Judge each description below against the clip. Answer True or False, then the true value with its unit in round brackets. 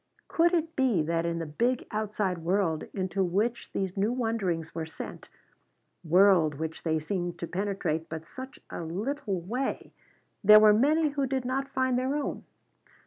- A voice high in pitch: True (200 Hz)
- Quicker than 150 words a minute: True (165 wpm)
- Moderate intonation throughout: False (7.2 semitones)